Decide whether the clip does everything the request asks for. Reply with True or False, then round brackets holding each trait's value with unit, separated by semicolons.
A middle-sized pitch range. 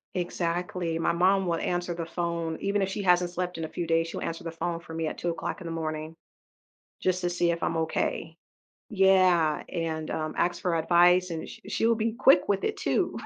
False (1.8 semitones)